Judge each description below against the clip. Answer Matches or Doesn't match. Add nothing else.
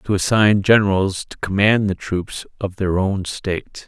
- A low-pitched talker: Matches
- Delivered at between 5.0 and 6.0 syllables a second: Doesn't match